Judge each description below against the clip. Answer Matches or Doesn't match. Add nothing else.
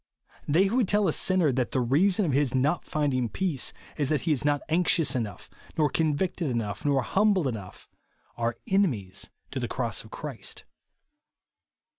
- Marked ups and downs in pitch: Matches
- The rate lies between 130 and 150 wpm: Doesn't match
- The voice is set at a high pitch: Doesn't match